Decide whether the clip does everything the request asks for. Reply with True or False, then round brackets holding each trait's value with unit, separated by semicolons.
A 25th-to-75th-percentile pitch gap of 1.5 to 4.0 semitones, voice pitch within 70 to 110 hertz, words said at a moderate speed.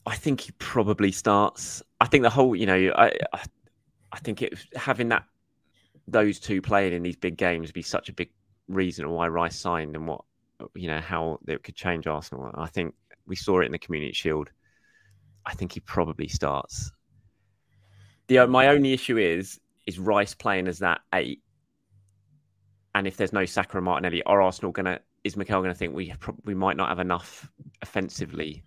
True (2.9 semitones; 95 Hz; 185 wpm)